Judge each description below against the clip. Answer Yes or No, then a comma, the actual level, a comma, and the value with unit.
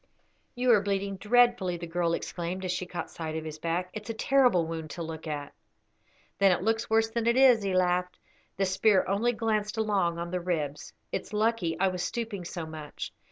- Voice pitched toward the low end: No, medium, 185 Hz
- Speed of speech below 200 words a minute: No, fast, 205 wpm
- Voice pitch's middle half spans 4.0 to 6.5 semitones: Yes, average, 4.5 semitones